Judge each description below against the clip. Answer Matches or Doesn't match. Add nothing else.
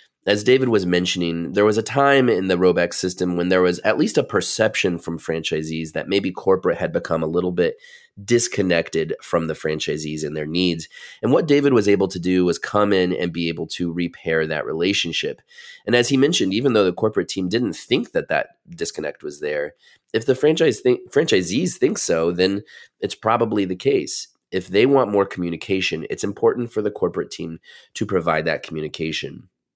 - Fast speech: Doesn't match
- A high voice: Doesn't match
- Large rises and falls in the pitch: Matches